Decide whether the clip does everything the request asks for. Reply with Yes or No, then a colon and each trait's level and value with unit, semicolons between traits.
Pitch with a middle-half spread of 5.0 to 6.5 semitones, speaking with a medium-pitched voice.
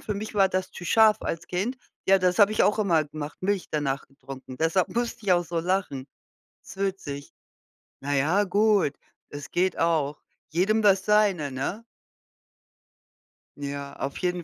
Yes: wide, 5.6 semitones; medium, 180 Hz